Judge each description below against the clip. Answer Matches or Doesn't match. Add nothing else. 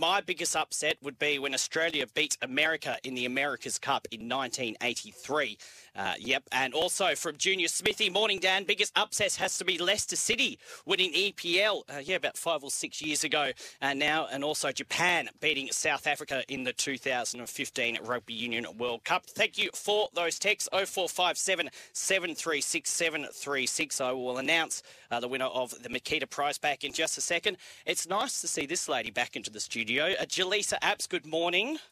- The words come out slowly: Doesn't match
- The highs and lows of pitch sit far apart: Matches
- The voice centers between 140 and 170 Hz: Matches